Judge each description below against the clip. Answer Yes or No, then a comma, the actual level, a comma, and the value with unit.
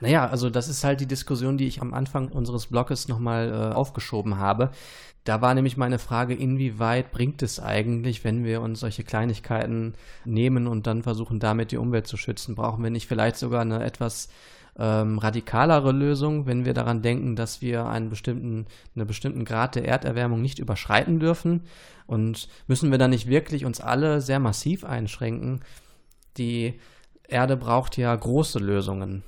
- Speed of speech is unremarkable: Yes, average, 170 wpm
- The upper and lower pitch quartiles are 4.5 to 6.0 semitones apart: No, narrow, 2.5 semitones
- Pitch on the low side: Yes, low, 120 Hz